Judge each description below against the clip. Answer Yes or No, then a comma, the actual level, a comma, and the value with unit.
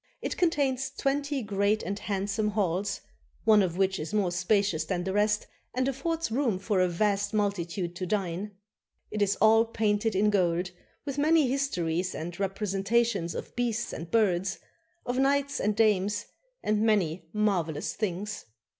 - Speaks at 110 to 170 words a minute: Yes, average, 155 wpm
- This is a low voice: No, high, 205 Hz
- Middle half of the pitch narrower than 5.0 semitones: Yes, average, 3.5 semitones